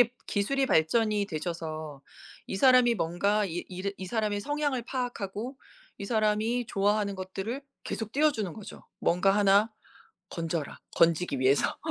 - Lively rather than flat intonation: No, average, 4.7 semitones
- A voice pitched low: No, high, 205 Hz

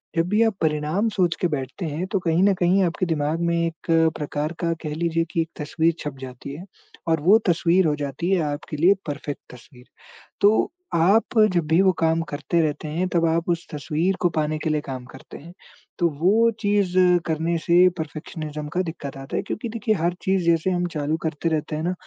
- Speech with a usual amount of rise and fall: Yes, average, 3.0 semitones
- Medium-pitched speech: Yes, medium, 165 Hz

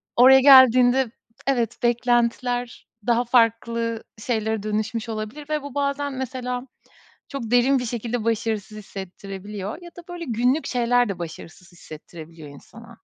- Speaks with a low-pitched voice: No, high, 235 Hz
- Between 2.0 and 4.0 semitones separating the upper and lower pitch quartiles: Yes, average, 2.9 semitones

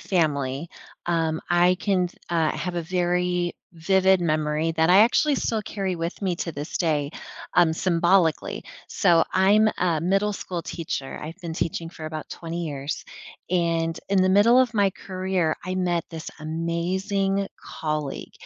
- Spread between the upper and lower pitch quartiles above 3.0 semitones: No, average, 2.7 semitones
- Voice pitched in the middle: Yes, medium, 175 Hz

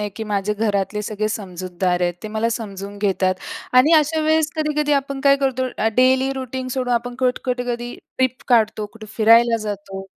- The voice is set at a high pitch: Yes, high, 230 Hz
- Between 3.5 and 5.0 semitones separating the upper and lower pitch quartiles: Yes, average, 4.1 semitones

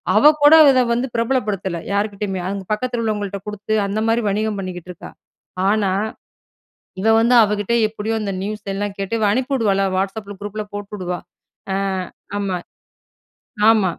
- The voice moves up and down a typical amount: No, narrow, 2.1 semitones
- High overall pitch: Yes, high, 210 Hz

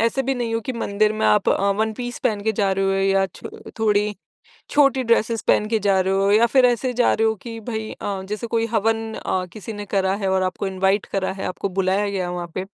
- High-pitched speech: Yes, high, 210 Hz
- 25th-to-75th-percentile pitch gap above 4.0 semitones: No, average, 2.7 semitones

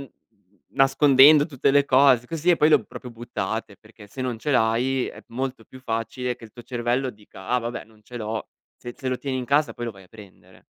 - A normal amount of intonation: Yes, average, 3.2 semitones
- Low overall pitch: Yes, low, 125 Hz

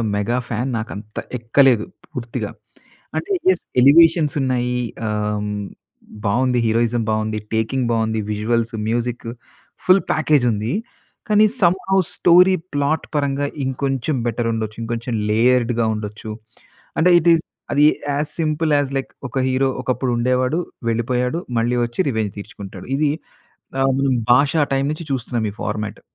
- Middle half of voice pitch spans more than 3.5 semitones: Yes, average, 4.1 semitones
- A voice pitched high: No, low, 125 Hz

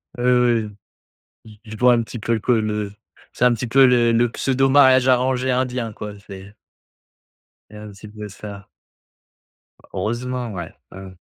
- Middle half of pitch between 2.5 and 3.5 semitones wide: Yes, average, 3.0 semitones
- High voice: No, low, 115 Hz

